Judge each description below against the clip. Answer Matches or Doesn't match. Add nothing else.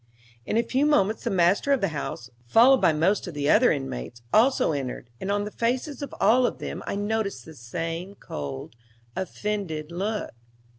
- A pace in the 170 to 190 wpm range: Matches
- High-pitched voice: Matches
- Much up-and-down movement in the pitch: Matches